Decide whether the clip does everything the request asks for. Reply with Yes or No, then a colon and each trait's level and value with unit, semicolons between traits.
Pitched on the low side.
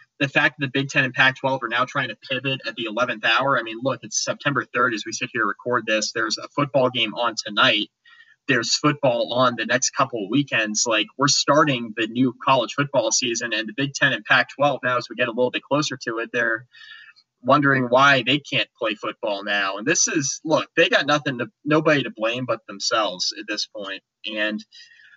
Yes: low, 130 Hz